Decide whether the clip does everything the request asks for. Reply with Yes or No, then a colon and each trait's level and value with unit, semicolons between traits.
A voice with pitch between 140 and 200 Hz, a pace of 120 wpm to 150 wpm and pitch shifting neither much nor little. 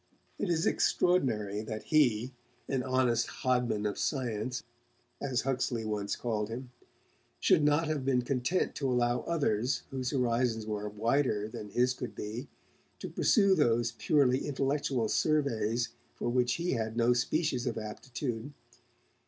No: low, 125 Hz; average, 140 wpm; average, 3.6 semitones